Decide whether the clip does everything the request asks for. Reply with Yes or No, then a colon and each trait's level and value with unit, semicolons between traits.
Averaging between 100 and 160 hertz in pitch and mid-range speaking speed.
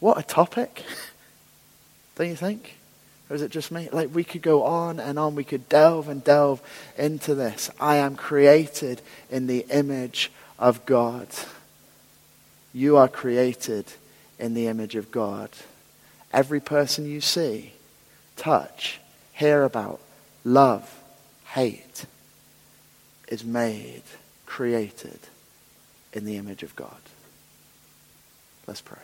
No: medium, 140 Hz; slow, 125 wpm